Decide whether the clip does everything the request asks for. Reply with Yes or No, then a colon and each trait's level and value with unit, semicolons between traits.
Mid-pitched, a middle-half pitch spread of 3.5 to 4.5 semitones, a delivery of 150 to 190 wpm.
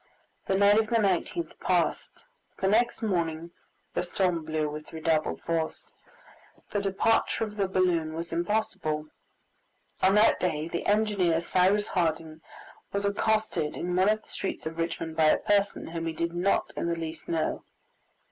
Yes: medium, 175 Hz; average, 3.8 semitones; average, 165 wpm